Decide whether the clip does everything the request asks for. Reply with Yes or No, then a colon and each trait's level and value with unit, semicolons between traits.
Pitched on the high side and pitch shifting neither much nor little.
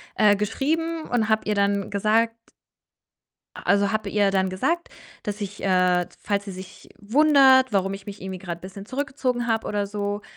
Yes: high, 205 Hz; average, 3.5 semitones